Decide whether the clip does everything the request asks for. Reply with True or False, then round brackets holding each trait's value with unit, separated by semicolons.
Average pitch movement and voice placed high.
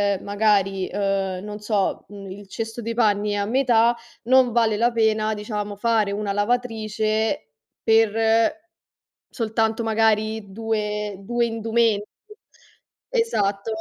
False (1.8 semitones; 215 Hz)